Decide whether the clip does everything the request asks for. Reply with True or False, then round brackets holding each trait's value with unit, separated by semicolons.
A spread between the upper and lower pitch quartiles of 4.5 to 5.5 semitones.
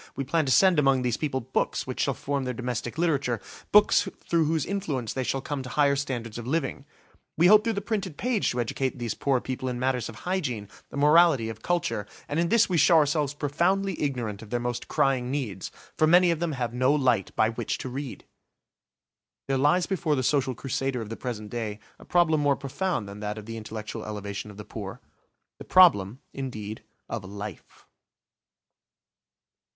True (5.2 semitones)